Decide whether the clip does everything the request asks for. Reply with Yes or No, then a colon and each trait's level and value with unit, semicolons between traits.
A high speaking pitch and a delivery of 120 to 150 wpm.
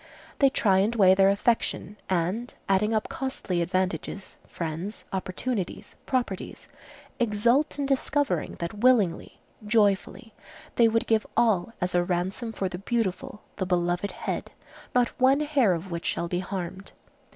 Yes: high, 200 Hz; average, 140 wpm